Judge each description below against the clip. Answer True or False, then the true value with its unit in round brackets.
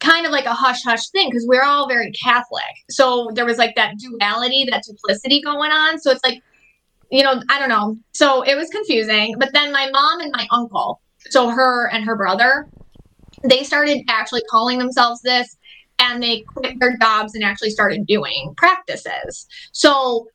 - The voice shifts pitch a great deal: False (3.3 semitones)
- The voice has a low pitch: False (250 Hz)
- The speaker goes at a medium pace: True (185 wpm)